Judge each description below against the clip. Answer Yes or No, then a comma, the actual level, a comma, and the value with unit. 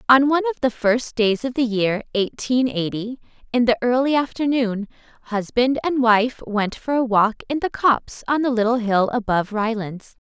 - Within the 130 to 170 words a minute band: No, average, 180 wpm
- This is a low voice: No, high, 240 Hz